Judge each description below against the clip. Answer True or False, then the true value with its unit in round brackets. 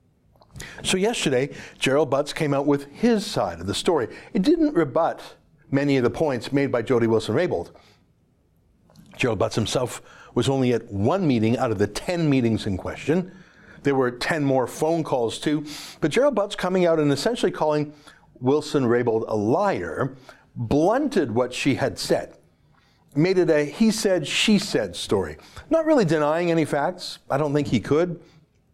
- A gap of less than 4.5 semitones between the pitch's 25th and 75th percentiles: False (4.9 semitones)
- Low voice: False (145 Hz)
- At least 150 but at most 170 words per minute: True (165 wpm)